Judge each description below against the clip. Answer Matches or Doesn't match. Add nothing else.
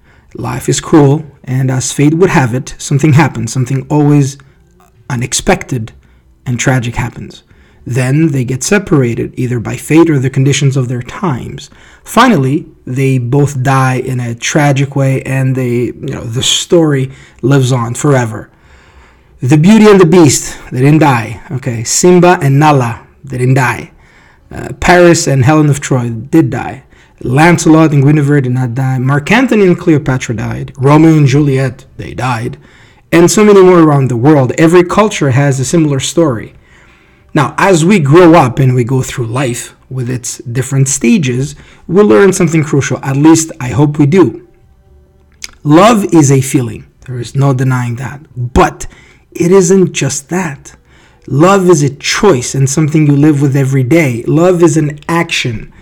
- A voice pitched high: Doesn't match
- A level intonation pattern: Doesn't match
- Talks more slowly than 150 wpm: Doesn't match